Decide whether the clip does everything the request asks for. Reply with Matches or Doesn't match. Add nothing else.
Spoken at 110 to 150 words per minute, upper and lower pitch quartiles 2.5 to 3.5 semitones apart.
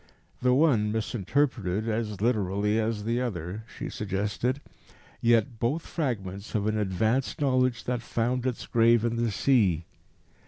Matches